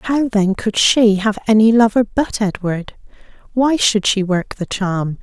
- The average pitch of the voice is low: No, high, 210 Hz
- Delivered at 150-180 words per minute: Yes, average, 170 wpm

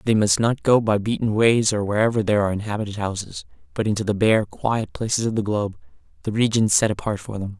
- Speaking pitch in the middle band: No, low, 105 Hz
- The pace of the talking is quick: Yes, fast, 215 wpm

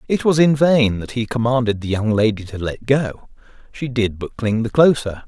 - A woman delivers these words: No, male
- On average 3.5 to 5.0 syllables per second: Yes, 4.9 syllables/s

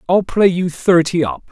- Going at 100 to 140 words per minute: No, average, 200 wpm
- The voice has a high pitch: No, medium, 170 Hz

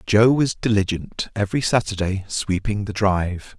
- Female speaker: No, male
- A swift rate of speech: No, slow, 135 wpm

